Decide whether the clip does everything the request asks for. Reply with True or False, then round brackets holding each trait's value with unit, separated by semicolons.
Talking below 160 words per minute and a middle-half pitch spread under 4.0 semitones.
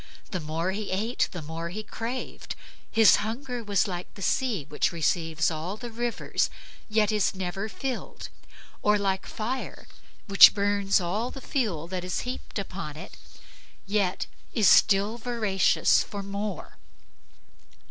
True (140 wpm; 3.5 semitones)